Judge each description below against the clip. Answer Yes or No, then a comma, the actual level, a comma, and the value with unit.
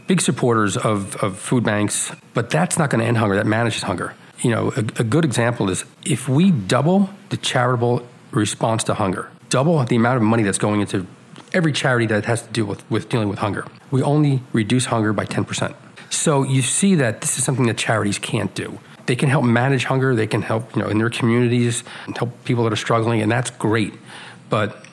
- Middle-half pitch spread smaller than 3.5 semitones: No, average, 3.8 semitones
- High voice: No, low, 120 Hz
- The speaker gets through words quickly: Yes, fast, 215 wpm